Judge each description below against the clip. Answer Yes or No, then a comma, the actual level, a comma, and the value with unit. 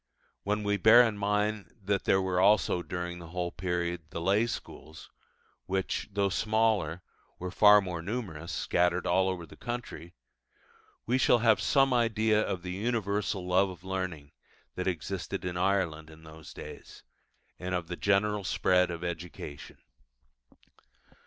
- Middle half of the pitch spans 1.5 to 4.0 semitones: Yes, average, 3.0 semitones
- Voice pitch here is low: Yes, very low, 95 Hz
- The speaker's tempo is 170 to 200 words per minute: No, average, 150 wpm